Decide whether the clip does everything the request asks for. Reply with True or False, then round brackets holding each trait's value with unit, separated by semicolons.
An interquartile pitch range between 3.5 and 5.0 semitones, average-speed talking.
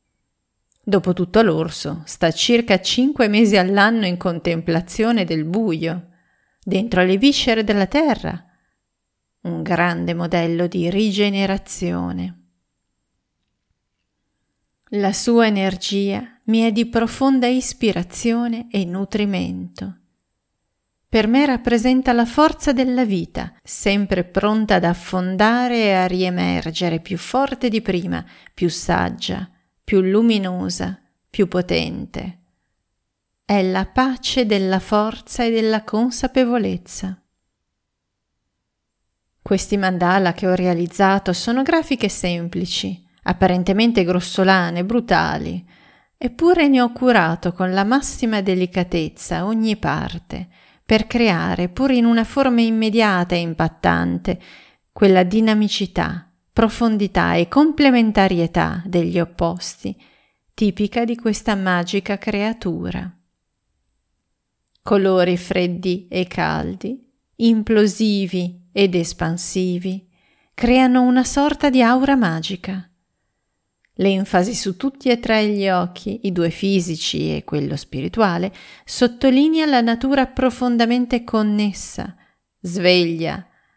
False (4.7 semitones; 100 wpm)